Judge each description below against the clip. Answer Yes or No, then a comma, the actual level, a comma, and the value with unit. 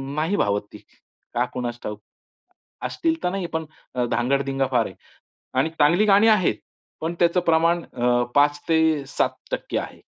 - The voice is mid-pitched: Yes, medium, 150 Hz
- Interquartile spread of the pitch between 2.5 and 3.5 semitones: No, wide, 5.5 semitones